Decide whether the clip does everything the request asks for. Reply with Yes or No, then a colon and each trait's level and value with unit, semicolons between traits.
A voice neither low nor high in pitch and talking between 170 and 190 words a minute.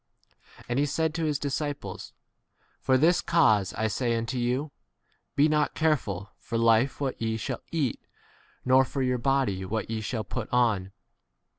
No: low, 125 Hz; average, 175 wpm